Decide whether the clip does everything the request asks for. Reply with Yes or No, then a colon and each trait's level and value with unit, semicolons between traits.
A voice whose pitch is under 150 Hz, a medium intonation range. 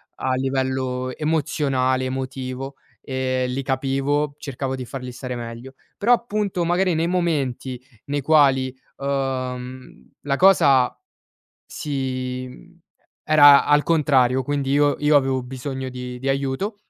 No: low, 135 Hz; narrow, 2.2 semitones